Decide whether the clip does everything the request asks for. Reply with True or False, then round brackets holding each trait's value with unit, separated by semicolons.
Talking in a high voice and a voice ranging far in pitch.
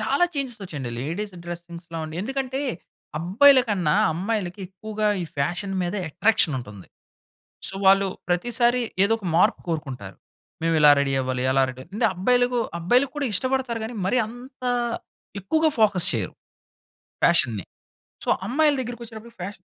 True (195 Hz; 6.6 semitones)